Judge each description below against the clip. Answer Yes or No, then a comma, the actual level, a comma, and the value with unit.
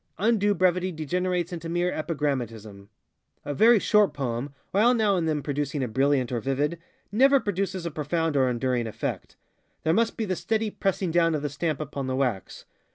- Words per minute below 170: No, average, 180 wpm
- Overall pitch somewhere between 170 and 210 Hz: No, medium, 160 Hz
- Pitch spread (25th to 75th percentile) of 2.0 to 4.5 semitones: No, wide, 5.5 semitones